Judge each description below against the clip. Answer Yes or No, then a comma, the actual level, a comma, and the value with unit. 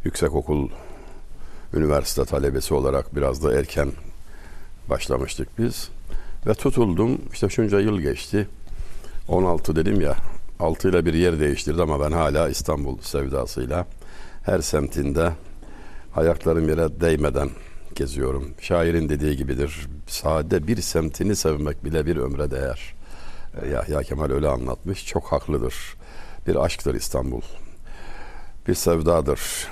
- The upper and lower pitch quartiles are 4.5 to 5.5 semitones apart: No, average, 3.4 semitones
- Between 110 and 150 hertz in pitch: No, very low, 80 Hz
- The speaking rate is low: No, average, 115 wpm